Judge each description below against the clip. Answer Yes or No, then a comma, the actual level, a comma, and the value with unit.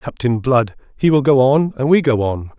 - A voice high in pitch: No, low, 130 Hz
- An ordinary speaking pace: No, fast, 230 wpm